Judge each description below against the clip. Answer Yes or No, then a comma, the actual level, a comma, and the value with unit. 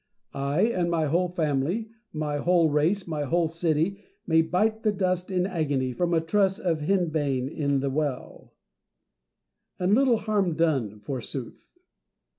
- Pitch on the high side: No, medium, 165 Hz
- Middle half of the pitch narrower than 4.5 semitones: Yes, average, 4.1 semitones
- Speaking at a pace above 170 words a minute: No, average, 145 wpm